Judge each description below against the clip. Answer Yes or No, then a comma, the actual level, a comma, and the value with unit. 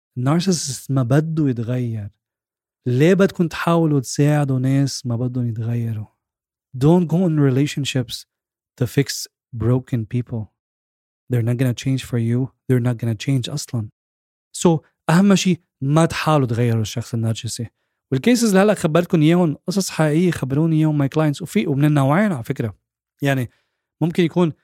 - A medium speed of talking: No, fast, 140 wpm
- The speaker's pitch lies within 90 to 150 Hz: Yes, low, 135 Hz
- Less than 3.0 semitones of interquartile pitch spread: No, average, 5.0 semitones